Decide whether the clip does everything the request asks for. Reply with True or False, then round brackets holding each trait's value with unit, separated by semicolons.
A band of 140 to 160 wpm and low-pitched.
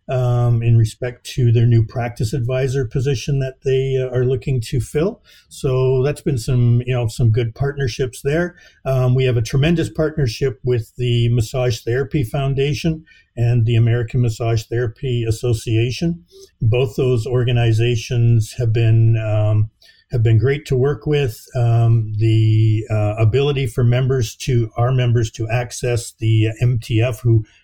True (150 wpm; 125 Hz)